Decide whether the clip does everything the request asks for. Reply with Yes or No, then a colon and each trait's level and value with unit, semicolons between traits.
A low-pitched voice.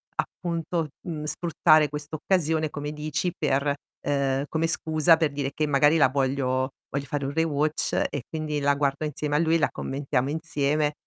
No: medium, 150 Hz